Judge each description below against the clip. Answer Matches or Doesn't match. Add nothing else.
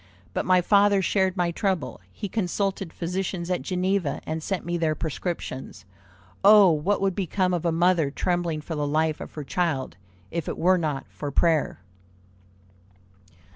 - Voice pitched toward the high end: Doesn't match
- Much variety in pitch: Doesn't match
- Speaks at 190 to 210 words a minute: Doesn't match